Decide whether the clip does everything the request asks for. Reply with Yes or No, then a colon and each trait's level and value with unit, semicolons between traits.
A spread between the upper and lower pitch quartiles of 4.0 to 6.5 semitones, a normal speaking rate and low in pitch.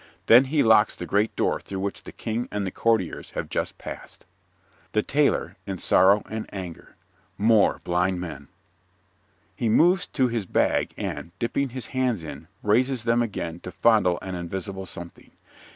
Yes: average, 4.5 semitones; average, 165 wpm; low, 105 Hz